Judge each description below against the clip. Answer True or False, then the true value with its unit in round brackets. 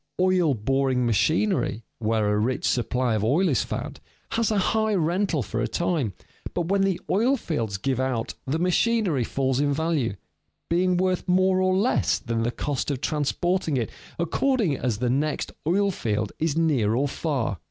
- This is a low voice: False (150 Hz)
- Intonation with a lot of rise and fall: True (7.1 semitones)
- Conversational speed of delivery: True (175 wpm)